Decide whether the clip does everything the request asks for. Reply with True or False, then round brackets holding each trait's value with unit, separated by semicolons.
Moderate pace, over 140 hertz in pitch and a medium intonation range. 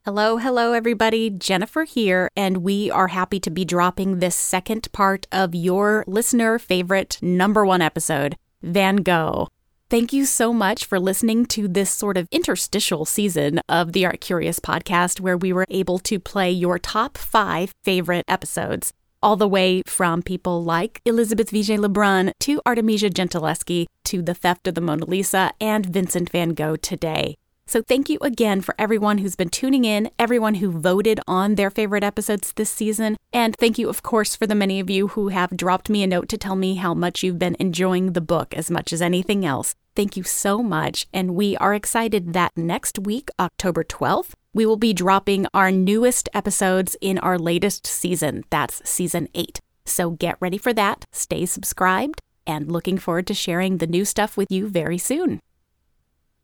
True (185 wpm; 190 Hz; 3.1 semitones)